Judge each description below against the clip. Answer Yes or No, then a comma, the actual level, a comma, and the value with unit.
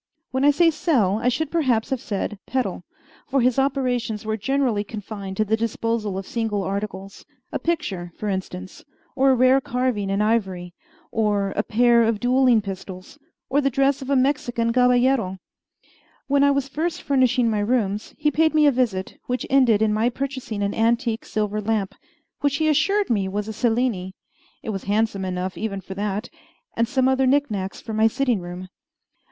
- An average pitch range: Yes, average, 4.5 semitones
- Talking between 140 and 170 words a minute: No, average, 180 wpm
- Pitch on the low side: No, high, 230 Hz